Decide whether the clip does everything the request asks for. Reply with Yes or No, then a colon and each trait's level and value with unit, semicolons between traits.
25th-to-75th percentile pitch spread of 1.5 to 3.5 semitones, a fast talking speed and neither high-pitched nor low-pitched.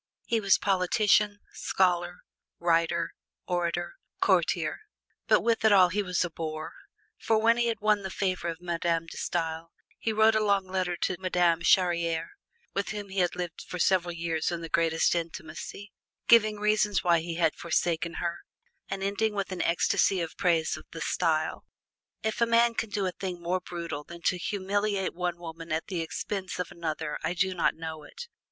No: average, 3.1 semitones; average, 185 wpm; medium, 180 Hz